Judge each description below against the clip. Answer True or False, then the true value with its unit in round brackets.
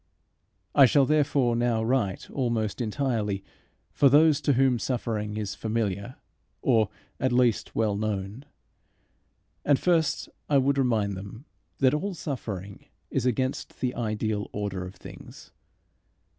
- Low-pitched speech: True (120 Hz)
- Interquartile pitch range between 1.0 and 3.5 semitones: False (4.3 semitones)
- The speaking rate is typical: False (130 wpm)